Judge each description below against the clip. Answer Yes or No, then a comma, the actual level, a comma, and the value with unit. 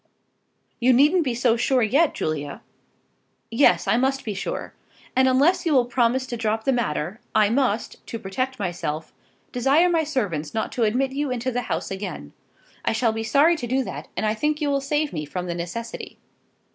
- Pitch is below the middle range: No, high, 245 Hz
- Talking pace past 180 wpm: Yes, average, 195 wpm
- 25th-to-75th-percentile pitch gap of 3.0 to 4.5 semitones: Yes, average, 4.2 semitones